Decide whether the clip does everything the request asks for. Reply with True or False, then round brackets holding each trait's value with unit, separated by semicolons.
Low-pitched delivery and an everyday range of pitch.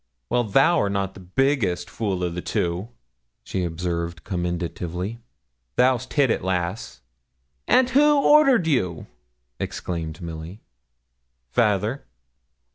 False (95 Hz; 6.5 semitones)